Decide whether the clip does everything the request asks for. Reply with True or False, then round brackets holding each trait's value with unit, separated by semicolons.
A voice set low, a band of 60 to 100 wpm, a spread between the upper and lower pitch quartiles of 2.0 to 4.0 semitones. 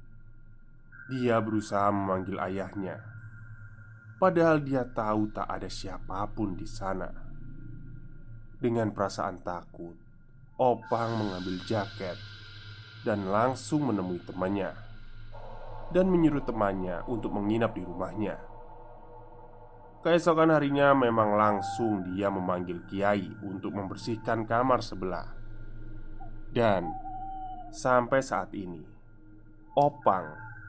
True (110 Hz; 90 wpm; 3.7 semitones)